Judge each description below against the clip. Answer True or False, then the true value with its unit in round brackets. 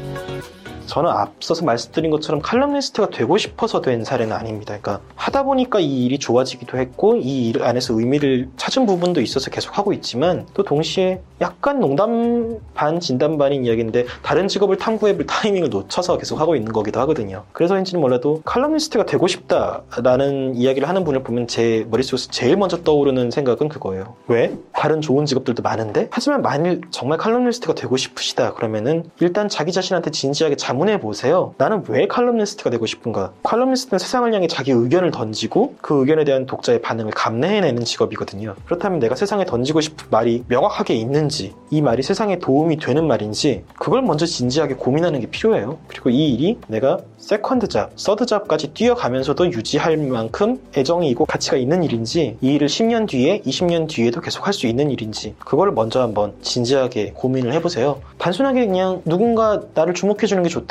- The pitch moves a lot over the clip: True (7.3 semitones)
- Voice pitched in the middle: True (150 Hz)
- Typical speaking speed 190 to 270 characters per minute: False (425 characters per minute)